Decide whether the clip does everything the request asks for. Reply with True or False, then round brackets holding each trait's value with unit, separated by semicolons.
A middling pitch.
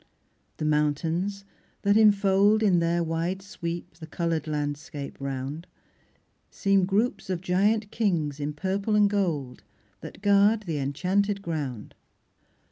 True (175 Hz)